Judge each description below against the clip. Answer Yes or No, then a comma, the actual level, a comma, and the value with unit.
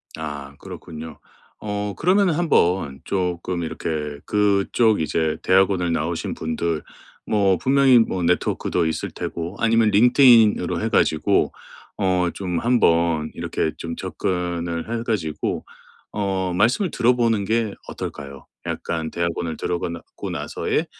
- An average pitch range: Yes, average, 4.8 semitones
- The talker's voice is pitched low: Yes, very low, 90 Hz